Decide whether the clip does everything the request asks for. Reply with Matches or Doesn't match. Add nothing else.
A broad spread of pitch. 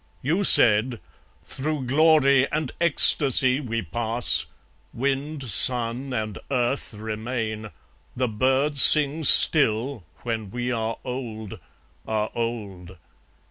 Doesn't match